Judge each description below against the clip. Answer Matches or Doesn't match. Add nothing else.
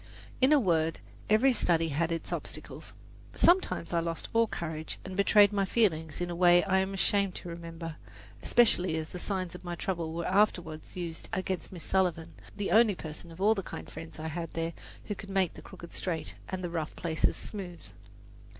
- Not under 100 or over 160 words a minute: Doesn't match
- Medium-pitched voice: Matches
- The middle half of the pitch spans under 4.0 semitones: Matches